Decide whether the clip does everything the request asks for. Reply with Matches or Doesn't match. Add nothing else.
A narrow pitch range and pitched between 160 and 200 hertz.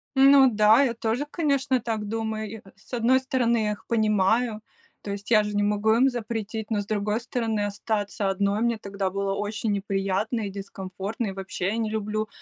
Doesn't match